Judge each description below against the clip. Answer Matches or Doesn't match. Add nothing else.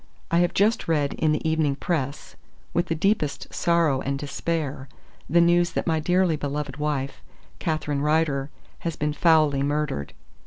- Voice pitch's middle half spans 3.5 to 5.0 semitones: Doesn't match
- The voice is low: Doesn't match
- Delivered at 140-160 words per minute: Matches